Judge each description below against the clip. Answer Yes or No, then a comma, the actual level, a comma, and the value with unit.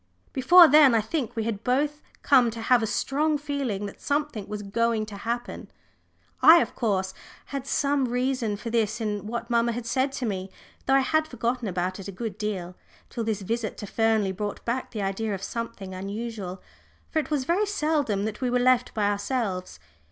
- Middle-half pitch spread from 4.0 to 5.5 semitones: Yes, average, 4.4 semitones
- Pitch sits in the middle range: No, high, 230 Hz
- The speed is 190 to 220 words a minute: Yes, average, 195 wpm